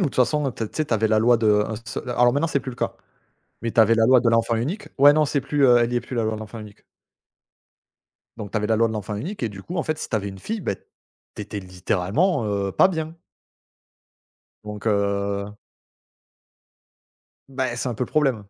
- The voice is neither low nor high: No, low, 115 Hz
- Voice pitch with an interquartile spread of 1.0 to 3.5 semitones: No, average, 4.6 semitones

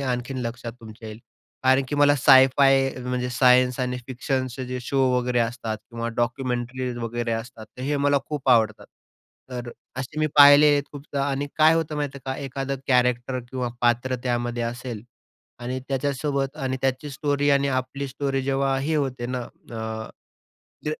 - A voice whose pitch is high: No, low, 130 Hz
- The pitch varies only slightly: Yes, narrow, 2.2 semitones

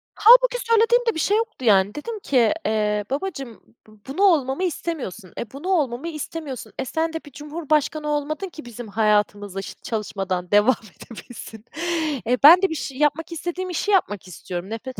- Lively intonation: Yes, wide, 7.8 semitones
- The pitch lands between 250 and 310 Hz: Yes, very high, 280 Hz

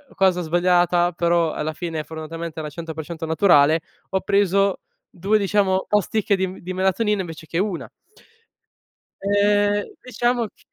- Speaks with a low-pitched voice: No, medium, 180 Hz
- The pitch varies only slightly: No, average, 3.4 semitones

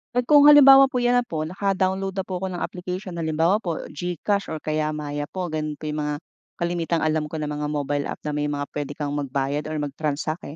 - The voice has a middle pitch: Yes, medium, 155 Hz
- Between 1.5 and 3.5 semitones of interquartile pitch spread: No, average, 4.0 semitones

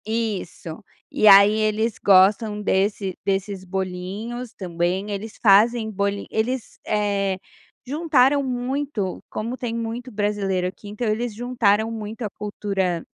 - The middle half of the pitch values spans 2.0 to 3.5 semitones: Yes, average, 3.0 semitones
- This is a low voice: No, high, 210 Hz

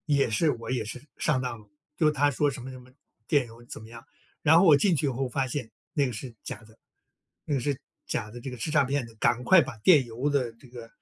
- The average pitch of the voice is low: Yes, low, 130 Hz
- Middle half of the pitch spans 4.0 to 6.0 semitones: No, average, 3.5 semitones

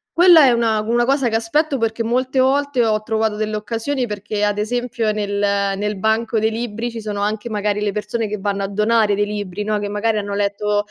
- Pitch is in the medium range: No, high, 215 Hz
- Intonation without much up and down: Yes, narrow, 2.2 semitones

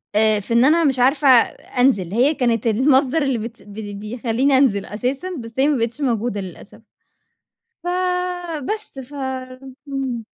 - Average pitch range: Yes, average, 3.5 semitones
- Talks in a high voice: Yes, very high, 250 Hz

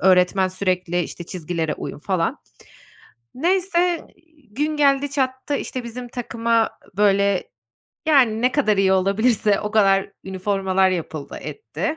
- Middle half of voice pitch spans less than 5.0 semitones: No, wide, 5.6 semitones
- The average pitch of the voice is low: No, high, 210 Hz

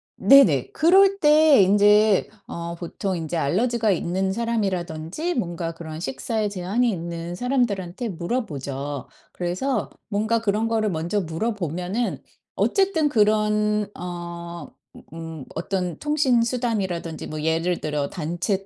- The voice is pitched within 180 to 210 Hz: Yes, high, 190 Hz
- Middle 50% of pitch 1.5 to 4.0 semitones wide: No, average, 5.3 semitones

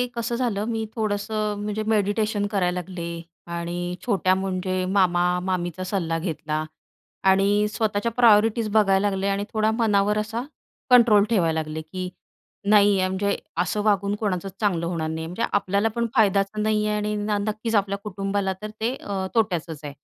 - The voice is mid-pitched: No, high, 200 Hz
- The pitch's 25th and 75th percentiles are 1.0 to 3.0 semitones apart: Yes, narrow, 2.6 semitones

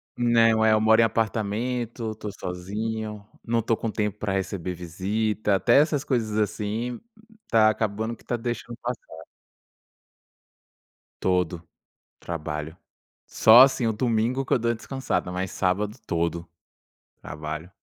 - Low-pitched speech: Yes, low, 110 Hz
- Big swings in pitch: No, average, 3.7 semitones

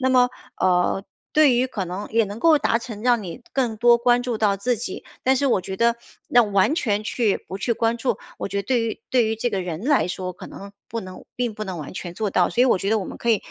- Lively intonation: No, average, 3.8 semitones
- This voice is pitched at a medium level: No, high, 225 Hz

